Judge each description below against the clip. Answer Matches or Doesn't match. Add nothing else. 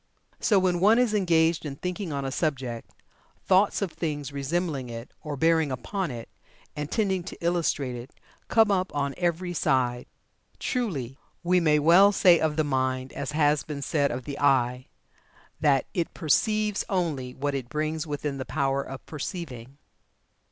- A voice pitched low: Doesn't match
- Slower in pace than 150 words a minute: Doesn't match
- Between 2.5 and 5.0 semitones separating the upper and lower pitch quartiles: Matches